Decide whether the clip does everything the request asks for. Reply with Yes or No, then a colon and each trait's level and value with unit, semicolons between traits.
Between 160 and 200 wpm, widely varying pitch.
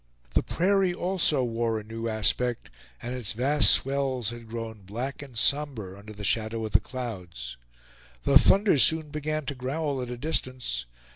No: average, 165 wpm; average, 4.5 semitones